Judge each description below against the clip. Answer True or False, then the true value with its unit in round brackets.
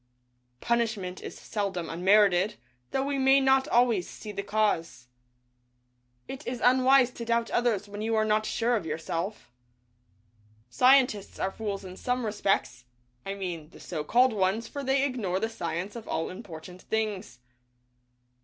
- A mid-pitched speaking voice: False (215 Hz)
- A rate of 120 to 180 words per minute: True (150 wpm)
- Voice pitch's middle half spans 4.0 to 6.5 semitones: True (4.6 semitones)